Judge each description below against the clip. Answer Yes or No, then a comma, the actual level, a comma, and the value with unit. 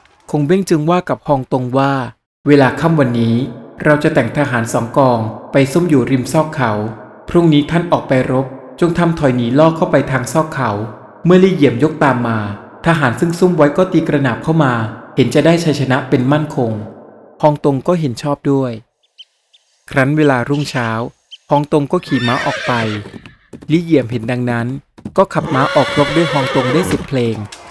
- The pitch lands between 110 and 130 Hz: No, medium, 140 Hz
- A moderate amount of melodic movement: Yes, average, 4.1 semitones